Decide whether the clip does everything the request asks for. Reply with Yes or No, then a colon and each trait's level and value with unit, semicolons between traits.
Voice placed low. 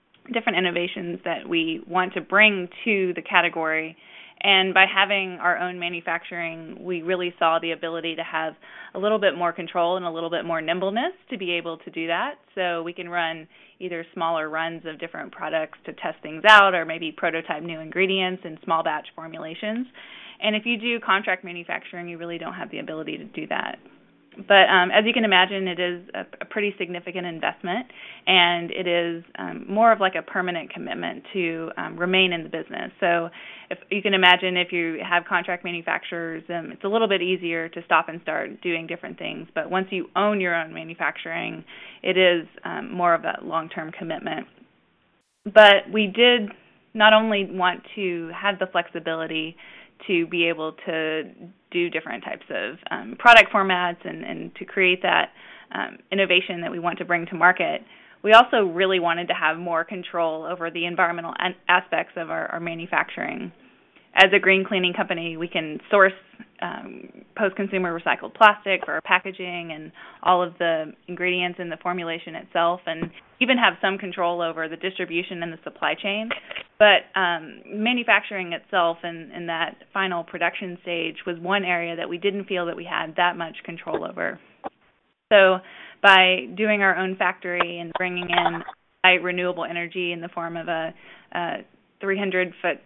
No: medium, 180 Hz